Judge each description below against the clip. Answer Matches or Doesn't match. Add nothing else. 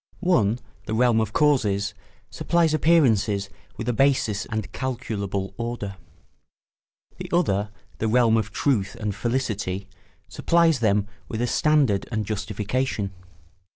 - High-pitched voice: Doesn't match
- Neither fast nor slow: Doesn't match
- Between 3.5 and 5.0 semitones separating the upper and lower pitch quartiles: Matches